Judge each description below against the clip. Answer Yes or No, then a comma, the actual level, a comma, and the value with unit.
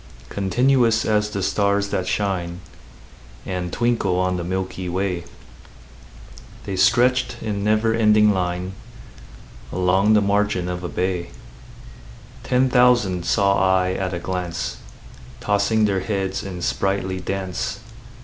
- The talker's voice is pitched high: No, very low, 95 Hz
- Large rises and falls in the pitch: No, narrow, 2.6 semitones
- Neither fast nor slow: No, slow, 120 wpm